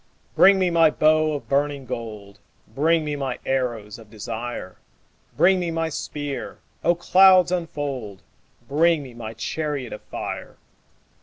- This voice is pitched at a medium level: Yes, medium, 145 Hz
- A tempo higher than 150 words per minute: No, average, 140 wpm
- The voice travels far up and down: Yes, wide, 5.7 semitones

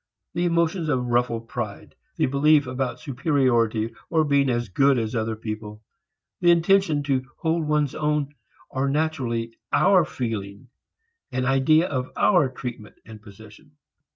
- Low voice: Yes, low, 130 Hz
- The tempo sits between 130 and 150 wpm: Yes, average, 140 wpm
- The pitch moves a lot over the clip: No, average, 4.8 semitones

